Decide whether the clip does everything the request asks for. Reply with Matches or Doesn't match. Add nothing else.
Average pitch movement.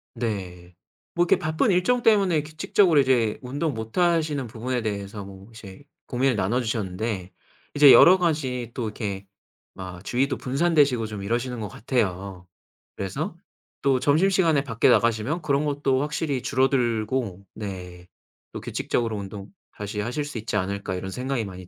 Doesn't match